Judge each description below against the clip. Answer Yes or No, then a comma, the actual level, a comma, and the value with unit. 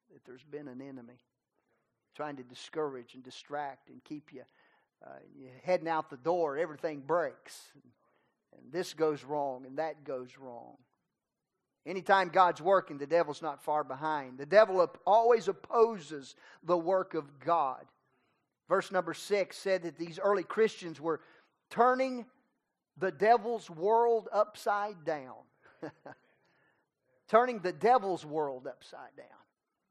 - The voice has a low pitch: No, medium, 165 Hz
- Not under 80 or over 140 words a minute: Yes, slow, 135 wpm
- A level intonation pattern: No, wide, 5.4 semitones